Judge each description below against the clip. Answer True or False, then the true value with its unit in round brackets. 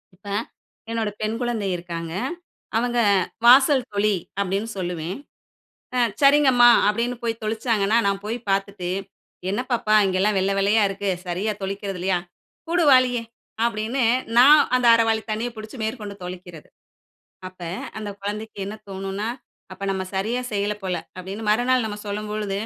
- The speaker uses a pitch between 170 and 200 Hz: False (210 Hz)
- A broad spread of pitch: False (3.1 semitones)